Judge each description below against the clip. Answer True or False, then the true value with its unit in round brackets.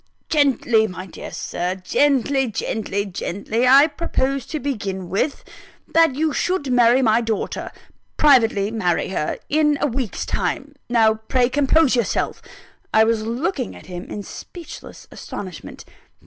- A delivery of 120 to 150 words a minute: True (135 wpm)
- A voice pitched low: False (240 Hz)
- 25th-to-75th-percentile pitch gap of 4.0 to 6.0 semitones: True (5.1 semitones)